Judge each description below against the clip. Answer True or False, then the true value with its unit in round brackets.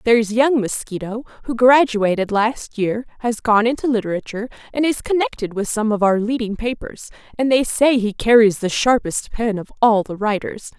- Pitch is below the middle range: False (225 Hz)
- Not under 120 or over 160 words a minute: False (180 wpm)